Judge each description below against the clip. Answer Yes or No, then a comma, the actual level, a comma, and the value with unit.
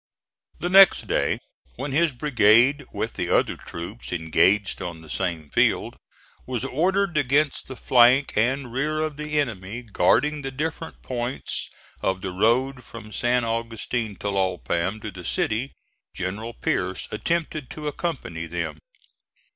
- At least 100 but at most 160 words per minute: Yes, average, 140 wpm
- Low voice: Yes, low, 120 Hz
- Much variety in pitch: Yes, wide, 7.0 semitones